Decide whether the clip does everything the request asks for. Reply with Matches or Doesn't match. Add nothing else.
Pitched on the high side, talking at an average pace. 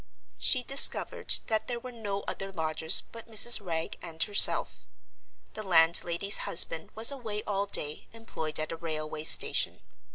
Matches